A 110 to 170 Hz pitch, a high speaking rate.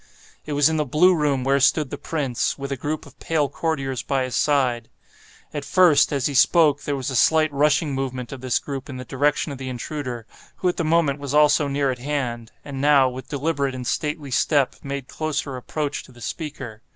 Yes: medium, 140 Hz; fast, 215 wpm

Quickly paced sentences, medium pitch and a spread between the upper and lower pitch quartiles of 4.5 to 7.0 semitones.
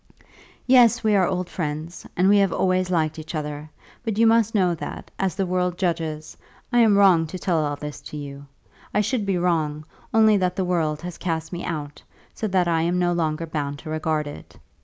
No: fast, 210 wpm; medium, 175 Hz; average, 3.6 semitones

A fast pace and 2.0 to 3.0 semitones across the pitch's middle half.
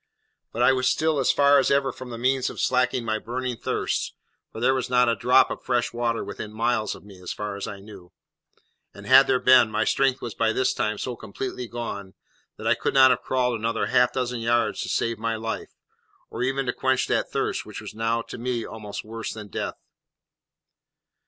Yes: fast, 215 wpm; narrow, 2.5 semitones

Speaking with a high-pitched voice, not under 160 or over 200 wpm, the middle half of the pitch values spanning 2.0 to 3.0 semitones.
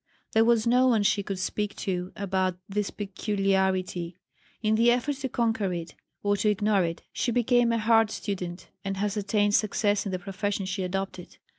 Yes: high, 205 Hz; average, 180 wpm; average, 2.7 semitones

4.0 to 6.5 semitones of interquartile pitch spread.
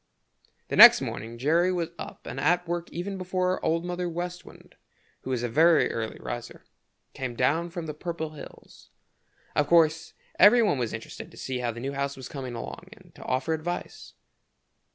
Yes: average, 5.2 semitones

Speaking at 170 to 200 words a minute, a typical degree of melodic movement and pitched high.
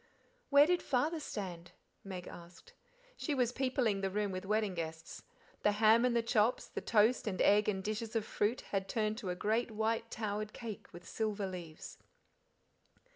Yes: average, 175 wpm; average, 3.3 semitones; high, 215 Hz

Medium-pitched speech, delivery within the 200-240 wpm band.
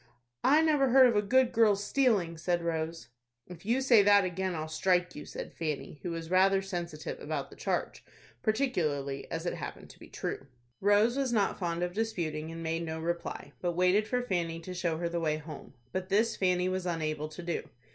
Yes: medium, 180 Hz; fast, 205 wpm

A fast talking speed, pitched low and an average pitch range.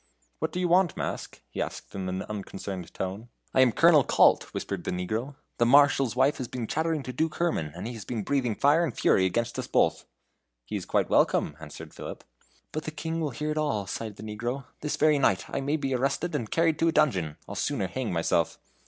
No: fast, 225 wpm; low, 125 Hz; wide, 7.0 semitones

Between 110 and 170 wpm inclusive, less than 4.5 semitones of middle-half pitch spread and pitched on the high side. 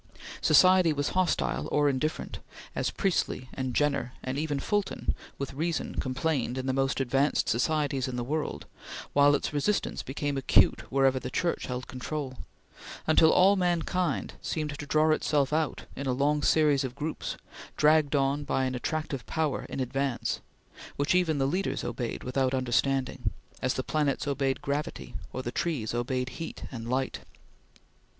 No: average, 160 wpm; average, 3.0 semitones; medium, 140 Hz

